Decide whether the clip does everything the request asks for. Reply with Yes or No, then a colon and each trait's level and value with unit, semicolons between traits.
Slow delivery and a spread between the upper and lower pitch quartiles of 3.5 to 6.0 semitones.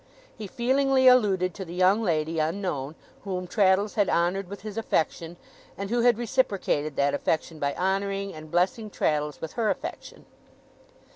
No: average, 155 wpm; average, 4.6 semitones